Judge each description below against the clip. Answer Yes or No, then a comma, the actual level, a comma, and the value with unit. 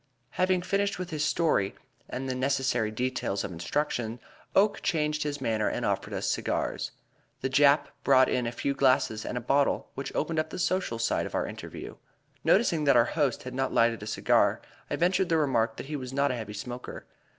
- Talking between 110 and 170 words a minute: No, average, 200 wpm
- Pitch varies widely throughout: No, average, 4.3 semitones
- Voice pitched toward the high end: No, low, 135 Hz